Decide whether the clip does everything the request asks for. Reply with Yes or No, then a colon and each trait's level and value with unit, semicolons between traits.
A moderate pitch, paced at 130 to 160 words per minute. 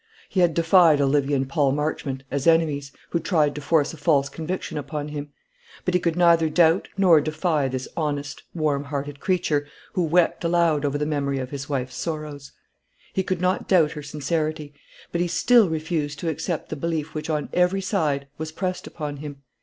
No: medium, 155 Hz; average, 190 wpm